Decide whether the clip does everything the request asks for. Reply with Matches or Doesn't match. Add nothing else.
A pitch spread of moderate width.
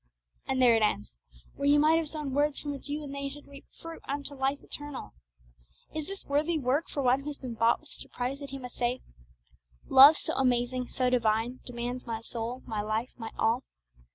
Matches